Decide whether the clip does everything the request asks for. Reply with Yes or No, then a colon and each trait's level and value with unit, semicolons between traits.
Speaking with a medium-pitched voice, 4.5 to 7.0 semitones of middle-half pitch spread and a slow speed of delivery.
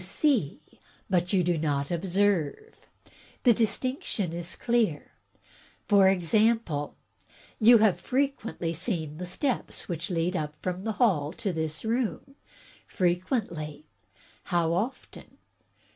Yes: medium, 180 Hz; average, 5.3 semitones; slow, 115 wpm